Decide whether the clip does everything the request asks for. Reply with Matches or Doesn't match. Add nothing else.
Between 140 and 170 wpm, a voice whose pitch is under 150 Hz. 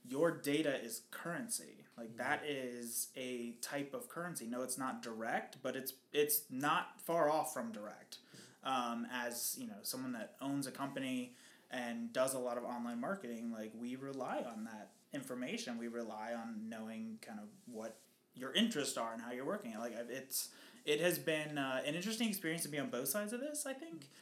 Doesn't match